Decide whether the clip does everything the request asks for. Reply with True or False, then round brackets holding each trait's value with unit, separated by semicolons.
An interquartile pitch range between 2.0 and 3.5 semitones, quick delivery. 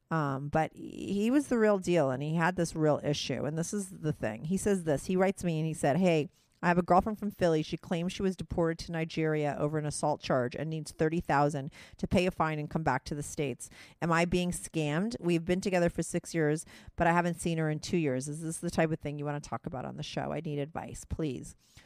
True (2.8 semitones; 260 wpm)